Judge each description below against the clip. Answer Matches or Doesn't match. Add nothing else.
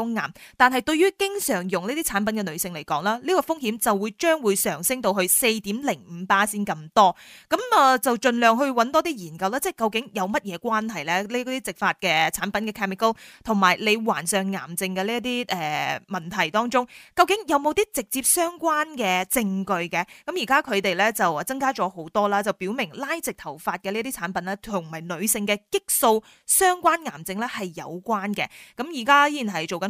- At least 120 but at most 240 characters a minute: Doesn't match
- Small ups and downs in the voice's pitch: Doesn't match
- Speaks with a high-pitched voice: Matches